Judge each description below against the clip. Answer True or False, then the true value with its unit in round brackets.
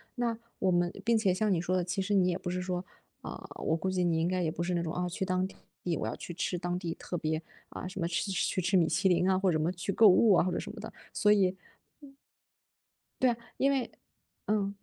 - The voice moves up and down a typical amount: False (2.1 semitones)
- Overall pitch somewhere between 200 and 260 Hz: False (185 Hz)